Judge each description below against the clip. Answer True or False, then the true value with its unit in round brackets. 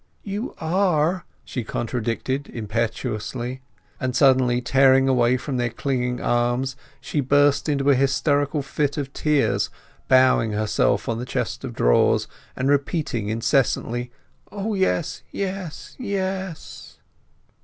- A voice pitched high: False (135 Hz)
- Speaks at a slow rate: True (120 wpm)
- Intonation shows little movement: False (3.7 semitones)